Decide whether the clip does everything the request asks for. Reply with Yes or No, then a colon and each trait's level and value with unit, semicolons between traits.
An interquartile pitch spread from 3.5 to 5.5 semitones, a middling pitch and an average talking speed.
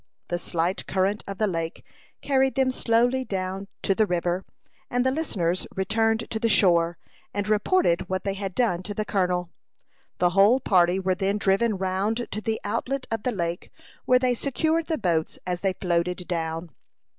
No: average, 4.2 semitones; high, 195 Hz; average, 180 wpm